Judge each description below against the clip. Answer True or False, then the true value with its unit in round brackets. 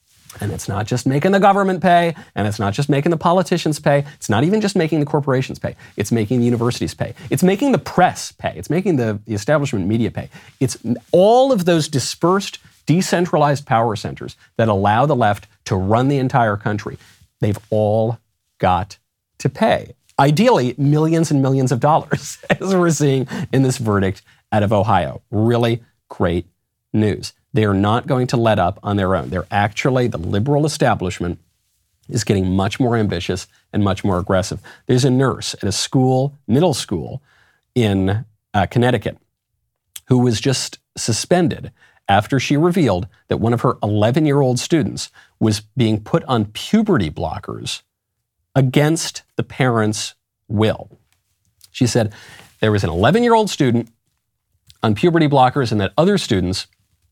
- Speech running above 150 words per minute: True (165 wpm)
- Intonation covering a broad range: True (5.8 semitones)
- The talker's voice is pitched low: True (120 Hz)